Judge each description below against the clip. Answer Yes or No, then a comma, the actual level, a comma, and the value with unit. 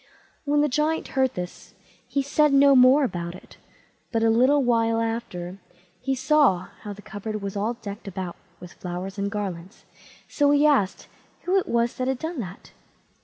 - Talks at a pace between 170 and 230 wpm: Yes, average, 175 wpm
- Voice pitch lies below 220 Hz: No, high, 230 Hz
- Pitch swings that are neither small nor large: No, wide, 5.9 semitones